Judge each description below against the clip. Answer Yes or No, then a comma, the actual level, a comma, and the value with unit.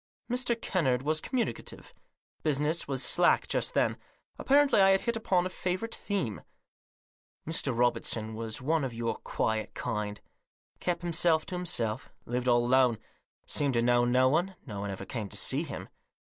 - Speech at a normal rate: Yes, average, 165 wpm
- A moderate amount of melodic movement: No, wide, 7.0 semitones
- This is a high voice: No, medium, 140 Hz